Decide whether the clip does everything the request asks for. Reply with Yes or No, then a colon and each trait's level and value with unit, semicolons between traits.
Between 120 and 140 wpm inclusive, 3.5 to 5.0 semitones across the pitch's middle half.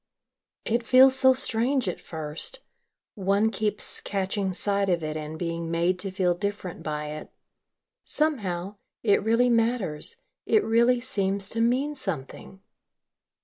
No: slow, 135 wpm; wide, 5.4 semitones